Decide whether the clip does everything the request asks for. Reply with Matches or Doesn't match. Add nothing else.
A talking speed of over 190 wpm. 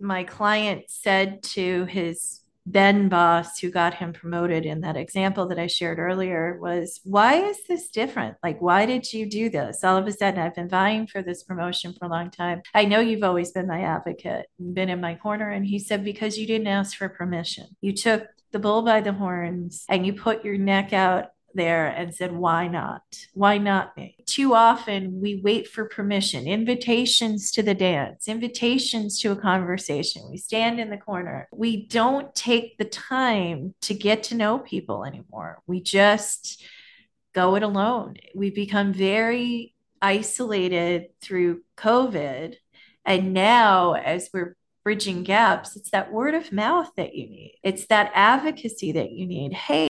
Doesn't match